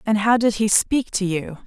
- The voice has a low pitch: No, high, 210 Hz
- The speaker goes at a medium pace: No, fast, 250 wpm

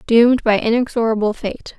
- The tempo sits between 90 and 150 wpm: Yes, slow, 135 wpm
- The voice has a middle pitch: No, high, 225 Hz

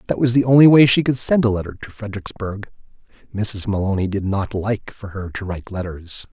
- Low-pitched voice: Yes, low, 105 Hz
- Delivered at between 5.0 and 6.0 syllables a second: Yes, 5.7 syllables/s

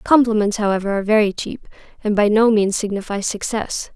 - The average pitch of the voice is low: No, high, 210 Hz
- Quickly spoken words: No, average, 165 wpm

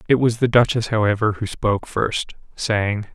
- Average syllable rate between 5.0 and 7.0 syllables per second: No, 4.8 syllables/s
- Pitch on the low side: Yes, low, 110 Hz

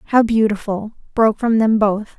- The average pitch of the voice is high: Yes, high, 215 Hz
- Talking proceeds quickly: No, average, 165 wpm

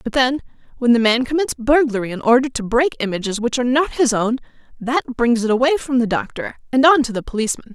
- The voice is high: Yes, very high, 250 Hz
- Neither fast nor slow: No, fast, 225 wpm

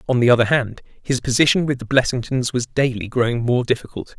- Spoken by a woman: No, male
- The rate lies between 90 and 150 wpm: No, average, 200 wpm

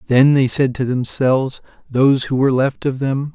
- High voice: No, low, 135 Hz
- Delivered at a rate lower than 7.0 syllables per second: Yes, 5.2 syllables/s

